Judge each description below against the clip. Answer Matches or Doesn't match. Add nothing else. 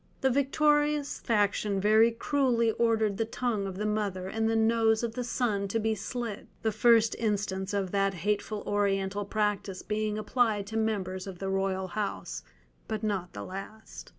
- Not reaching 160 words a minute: Doesn't match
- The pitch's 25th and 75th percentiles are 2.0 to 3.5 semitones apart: Matches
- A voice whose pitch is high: Matches